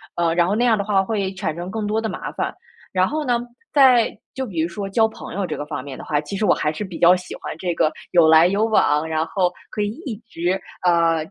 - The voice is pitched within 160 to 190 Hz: Yes, medium, 185 Hz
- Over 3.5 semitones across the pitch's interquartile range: Yes, average, 4.5 semitones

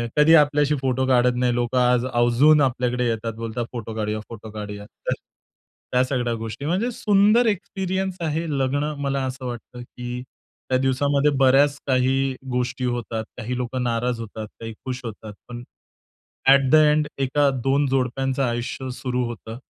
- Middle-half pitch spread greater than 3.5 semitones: No, average, 2.8 semitones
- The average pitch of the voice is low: Yes, low, 125 Hz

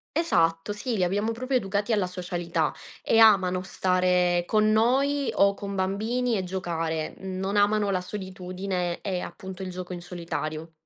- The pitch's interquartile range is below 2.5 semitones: No, average, 2.8 semitones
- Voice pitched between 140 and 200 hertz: Yes, high, 190 Hz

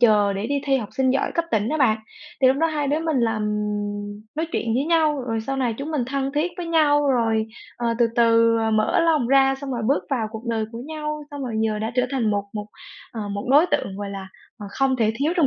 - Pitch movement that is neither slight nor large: Yes, average, 4.8 semitones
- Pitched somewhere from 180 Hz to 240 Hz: No, very high, 255 Hz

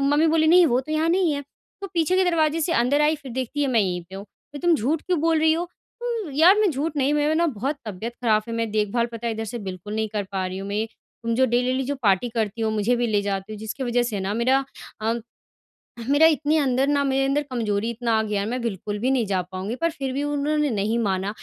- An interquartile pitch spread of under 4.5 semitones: No, wide, 5.6 semitones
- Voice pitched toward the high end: Yes, high, 245 Hz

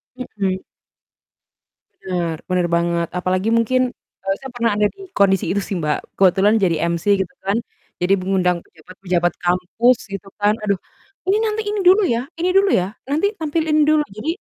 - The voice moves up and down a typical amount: No, wide, 6.0 semitones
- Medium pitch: No, high, 195 Hz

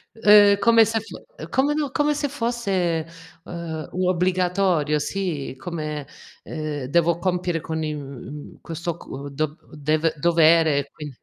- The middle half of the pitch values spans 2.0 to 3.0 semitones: No, average, 4.4 semitones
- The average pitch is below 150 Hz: No, medium, 170 Hz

